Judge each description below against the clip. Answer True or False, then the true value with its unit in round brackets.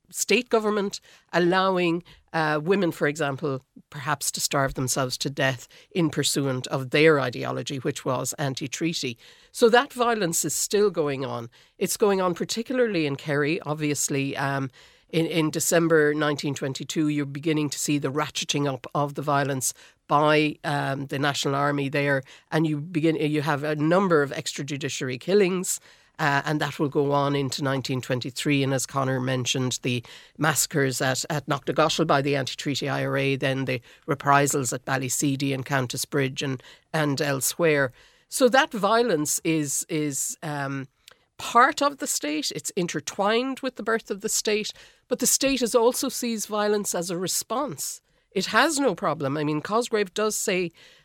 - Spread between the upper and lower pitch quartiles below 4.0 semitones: False (4.6 semitones)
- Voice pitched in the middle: True (150 Hz)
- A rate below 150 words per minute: False (160 wpm)